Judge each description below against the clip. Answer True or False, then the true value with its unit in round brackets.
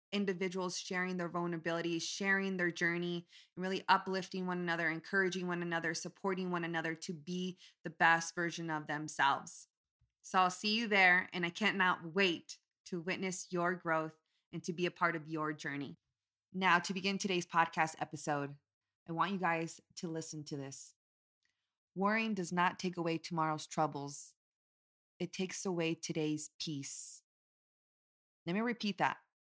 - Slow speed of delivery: False (155 wpm)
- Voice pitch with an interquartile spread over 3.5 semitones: False (2.7 semitones)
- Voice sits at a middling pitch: True (170 Hz)